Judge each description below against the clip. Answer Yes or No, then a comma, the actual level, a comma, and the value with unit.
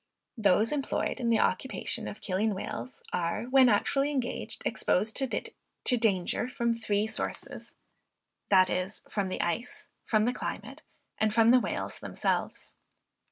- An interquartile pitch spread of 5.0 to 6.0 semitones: No, average, 4.1 semitones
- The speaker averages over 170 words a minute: No, slow, 135 wpm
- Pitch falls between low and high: No, high, 220 Hz